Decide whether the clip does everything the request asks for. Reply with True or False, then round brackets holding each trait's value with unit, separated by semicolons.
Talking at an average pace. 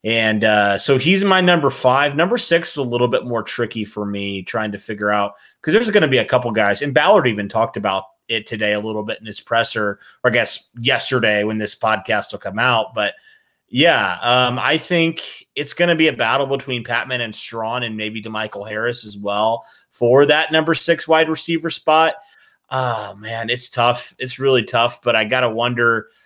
False (210 wpm)